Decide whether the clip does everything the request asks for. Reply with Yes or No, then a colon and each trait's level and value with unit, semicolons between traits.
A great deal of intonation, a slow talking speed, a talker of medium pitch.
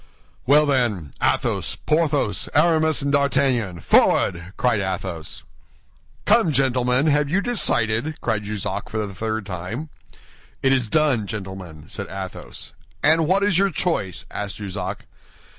No: wide, 7.4 semitones; slow, 130 wpm; low, 120 Hz